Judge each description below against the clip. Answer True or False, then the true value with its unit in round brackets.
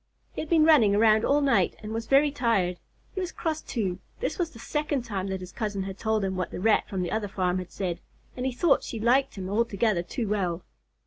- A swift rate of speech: True (240 wpm)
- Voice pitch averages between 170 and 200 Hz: False (220 Hz)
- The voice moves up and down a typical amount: False (6.0 semitones)